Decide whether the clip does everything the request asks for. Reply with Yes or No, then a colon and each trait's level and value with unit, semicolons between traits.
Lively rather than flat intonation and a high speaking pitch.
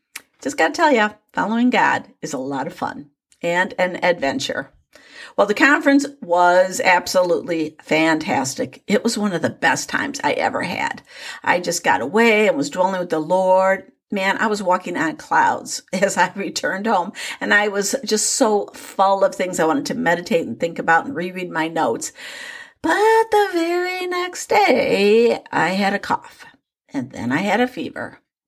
Yes: wide, 6.6 semitones; high, 200 Hz